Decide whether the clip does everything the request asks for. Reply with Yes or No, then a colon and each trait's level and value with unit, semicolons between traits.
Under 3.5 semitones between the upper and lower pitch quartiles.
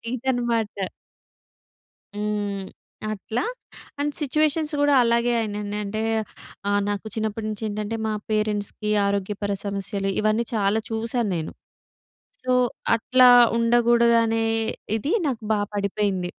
Yes: narrow, 2.5 semitones